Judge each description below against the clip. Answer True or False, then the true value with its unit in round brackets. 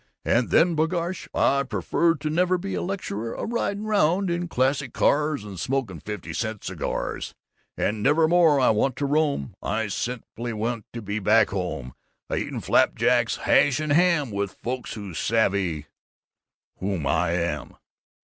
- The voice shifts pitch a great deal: True (7.6 semitones)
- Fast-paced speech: False (165 wpm)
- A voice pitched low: True (125 Hz)